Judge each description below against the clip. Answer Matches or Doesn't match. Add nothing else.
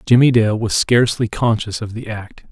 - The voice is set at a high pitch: Doesn't match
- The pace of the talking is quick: Doesn't match